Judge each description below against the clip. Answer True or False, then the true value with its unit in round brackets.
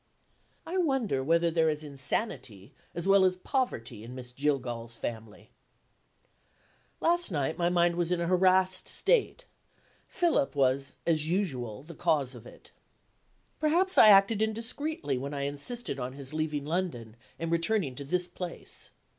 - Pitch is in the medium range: True (165 Hz)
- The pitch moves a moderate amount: False (6.4 semitones)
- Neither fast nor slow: True (145 wpm)